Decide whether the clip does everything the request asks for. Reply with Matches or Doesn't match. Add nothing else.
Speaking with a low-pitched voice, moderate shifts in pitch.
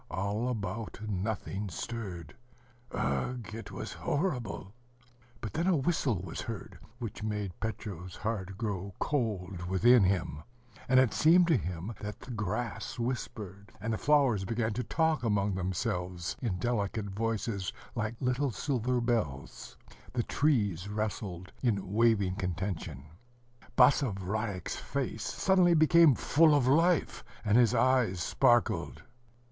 Matches